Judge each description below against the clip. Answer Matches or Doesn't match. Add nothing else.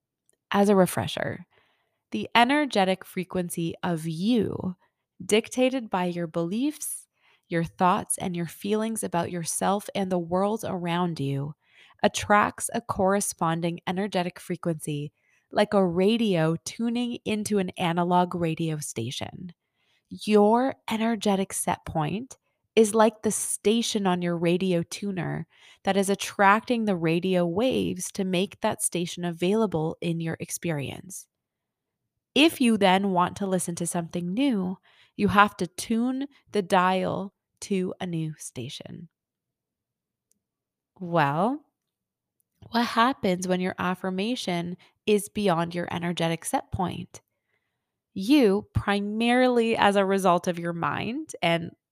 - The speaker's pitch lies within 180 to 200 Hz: Matches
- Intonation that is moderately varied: Matches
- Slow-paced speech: Matches